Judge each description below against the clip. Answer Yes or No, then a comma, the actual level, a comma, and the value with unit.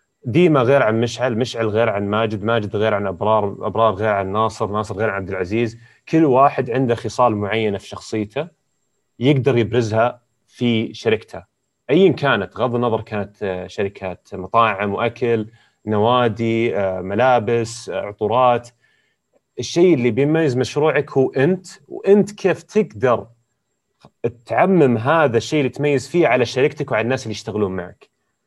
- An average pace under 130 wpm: No, fast, 135 wpm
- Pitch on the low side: Yes, low, 115 Hz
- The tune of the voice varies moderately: Yes, average, 3.5 semitones